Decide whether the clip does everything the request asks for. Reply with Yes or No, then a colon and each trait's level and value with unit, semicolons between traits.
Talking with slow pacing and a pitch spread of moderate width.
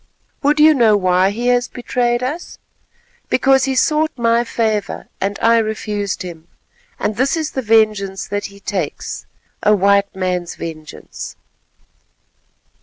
Yes: slow, 130 wpm; average, 3.9 semitones